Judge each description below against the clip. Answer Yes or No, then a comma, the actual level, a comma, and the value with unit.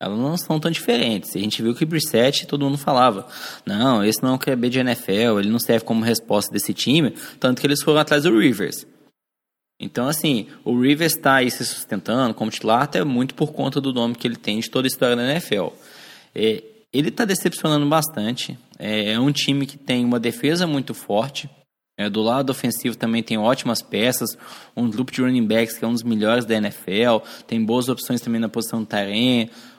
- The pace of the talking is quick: Yes, fast, 210 wpm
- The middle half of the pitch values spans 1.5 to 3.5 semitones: No, average, 3.9 semitones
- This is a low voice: Yes, low, 125 Hz